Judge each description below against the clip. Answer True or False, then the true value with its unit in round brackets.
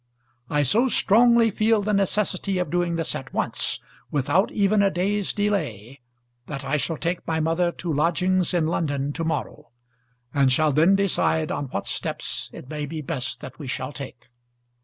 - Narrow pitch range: False (5.4 semitones)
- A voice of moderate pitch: True (165 Hz)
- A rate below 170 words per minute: False (175 wpm)